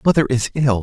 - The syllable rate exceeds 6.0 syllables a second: No, 5.9 syllables/s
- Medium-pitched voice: No, low, 130 Hz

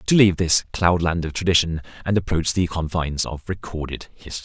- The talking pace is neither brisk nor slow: Yes, average, 175 wpm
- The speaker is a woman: No, male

